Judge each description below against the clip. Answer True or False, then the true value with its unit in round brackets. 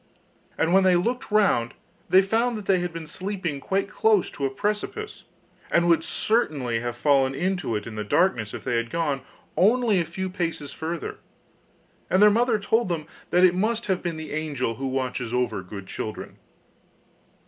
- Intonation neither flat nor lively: False (6.6 semitones)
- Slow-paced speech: False (180 wpm)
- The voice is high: False (170 Hz)